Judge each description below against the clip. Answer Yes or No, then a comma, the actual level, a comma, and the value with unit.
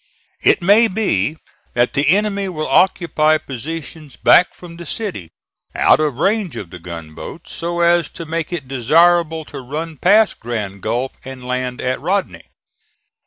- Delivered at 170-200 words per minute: No, average, 155 wpm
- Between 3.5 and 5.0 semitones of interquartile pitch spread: No, wide, 5.5 semitones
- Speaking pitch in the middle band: Yes, medium, 155 Hz